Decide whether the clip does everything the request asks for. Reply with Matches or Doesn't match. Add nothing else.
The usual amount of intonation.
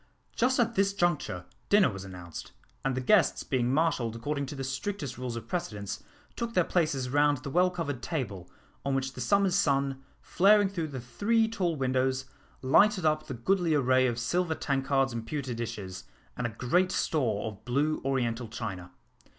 Doesn't match